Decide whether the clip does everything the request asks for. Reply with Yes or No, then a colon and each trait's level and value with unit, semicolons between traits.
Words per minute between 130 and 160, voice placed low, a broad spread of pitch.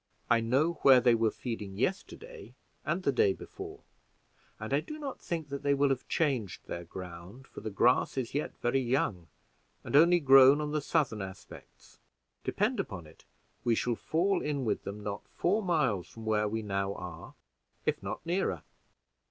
No: average, 175 wpm; low, 130 Hz; wide, 7.4 semitones